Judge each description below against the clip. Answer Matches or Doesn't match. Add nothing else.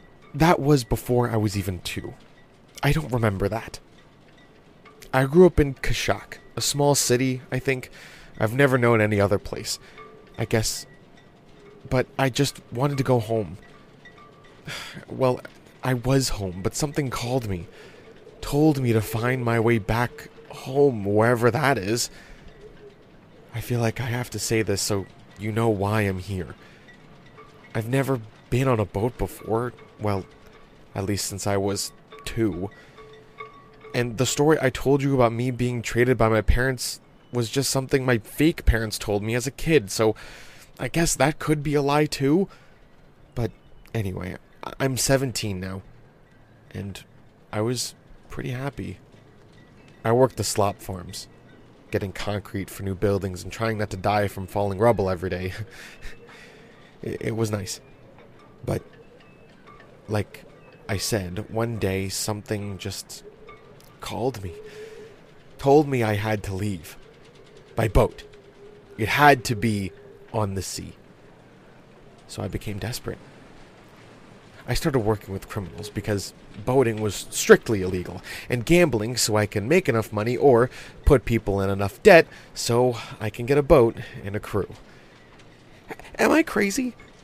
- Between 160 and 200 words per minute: Doesn't match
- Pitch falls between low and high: Doesn't match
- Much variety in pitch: Doesn't match